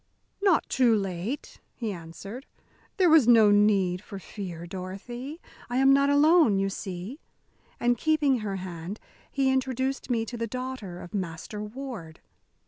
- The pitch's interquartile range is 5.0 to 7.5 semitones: Yes, wide, 5.6 semitones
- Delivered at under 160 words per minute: Yes, average, 145 wpm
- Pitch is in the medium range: No, high, 225 Hz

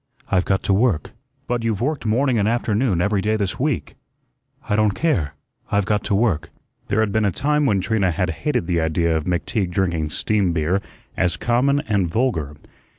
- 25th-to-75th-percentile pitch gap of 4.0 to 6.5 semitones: Yes, average, 4.9 semitones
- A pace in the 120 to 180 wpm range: No, average, 190 wpm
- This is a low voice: Yes, low, 100 Hz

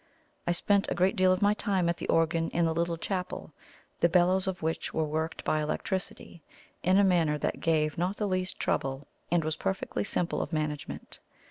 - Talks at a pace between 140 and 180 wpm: No, average, 200 wpm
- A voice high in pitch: No, medium, 170 Hz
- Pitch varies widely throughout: No, average, 2.8 semitones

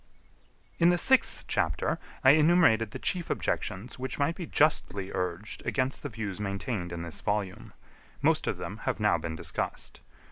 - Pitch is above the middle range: No, low, 110 Hz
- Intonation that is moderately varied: No, wide, 8.3 semitones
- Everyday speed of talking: Yes, average, 165 wpm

